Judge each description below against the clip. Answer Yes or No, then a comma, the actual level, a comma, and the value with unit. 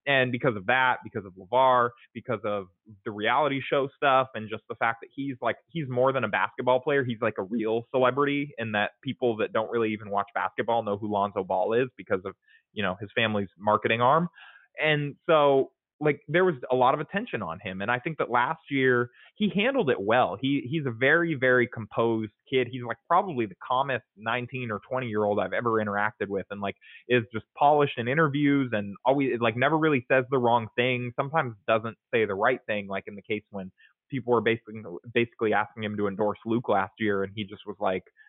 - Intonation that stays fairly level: No, average, 4.1 semitones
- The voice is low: Yes, low, 120 Hz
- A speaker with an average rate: No, fast, 215 wpm